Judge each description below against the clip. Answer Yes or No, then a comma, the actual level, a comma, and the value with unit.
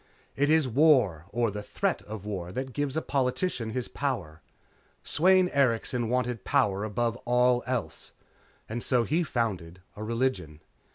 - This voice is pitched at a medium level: No, low, 120 Hz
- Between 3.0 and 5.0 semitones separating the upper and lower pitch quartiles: Yes, average, 3.9 semitones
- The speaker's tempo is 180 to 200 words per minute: No, average, 150 wpm